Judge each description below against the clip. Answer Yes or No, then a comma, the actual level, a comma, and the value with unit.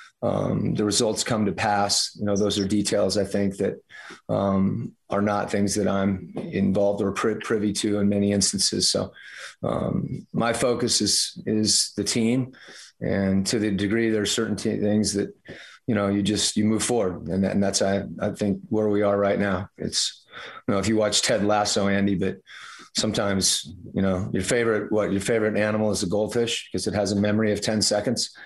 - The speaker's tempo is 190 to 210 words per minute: Yes, average, 200 wpm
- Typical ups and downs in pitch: No, narrow, 1.2 semitones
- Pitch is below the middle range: Yes, low, 105 Hz